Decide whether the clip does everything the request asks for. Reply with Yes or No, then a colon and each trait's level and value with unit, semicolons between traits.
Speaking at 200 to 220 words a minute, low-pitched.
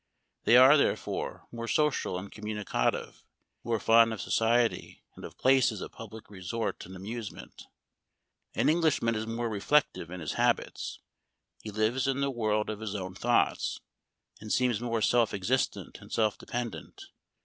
No: average, 155 wpm; low, 115 Hz